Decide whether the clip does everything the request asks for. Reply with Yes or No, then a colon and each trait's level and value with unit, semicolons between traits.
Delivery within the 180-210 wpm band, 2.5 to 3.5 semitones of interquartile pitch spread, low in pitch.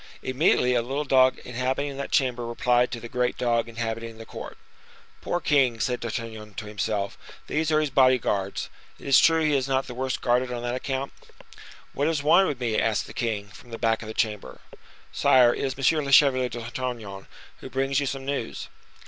Yes: average, 200 wpm; average, 2.8 semitones; low, 125 Hz